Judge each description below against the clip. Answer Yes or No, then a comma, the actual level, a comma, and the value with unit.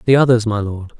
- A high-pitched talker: No, low, 115 Hz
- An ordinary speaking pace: No, fast, 240 wpm